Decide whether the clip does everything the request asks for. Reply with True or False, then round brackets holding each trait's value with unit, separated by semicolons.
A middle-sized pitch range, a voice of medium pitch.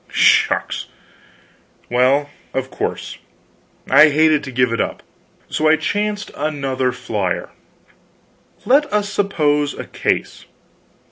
True (3.6 semitones; 145 Hz)